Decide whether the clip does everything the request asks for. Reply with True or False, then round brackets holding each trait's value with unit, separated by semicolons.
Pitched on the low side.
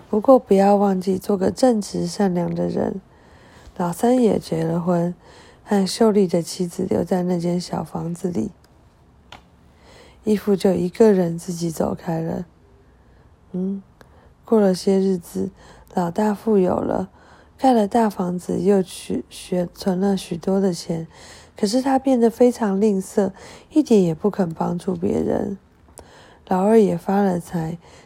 False (190 Hz)